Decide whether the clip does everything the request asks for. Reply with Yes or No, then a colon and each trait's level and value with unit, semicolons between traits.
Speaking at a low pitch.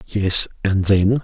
Yes: low, 100 Hz